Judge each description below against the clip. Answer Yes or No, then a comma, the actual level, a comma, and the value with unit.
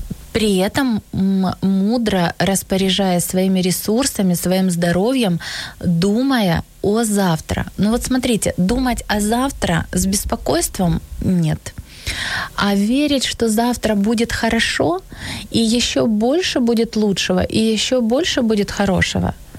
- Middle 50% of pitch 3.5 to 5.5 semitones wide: Yes, average, 4.2 semitones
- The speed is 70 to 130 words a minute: Yes, average, 110 wpm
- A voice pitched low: No, high, 205 Hz